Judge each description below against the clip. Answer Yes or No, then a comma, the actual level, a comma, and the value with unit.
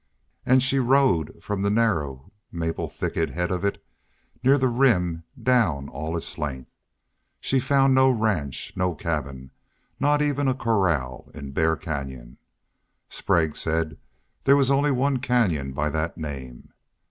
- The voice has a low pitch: Yes, very low, 90 Hz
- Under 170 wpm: Yes, average, 145 wpm